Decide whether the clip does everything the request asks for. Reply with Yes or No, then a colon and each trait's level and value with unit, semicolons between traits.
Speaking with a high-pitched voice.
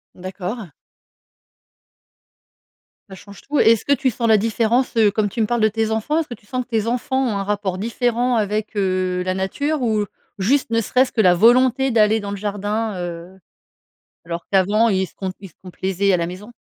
Yes: high, 215 Hz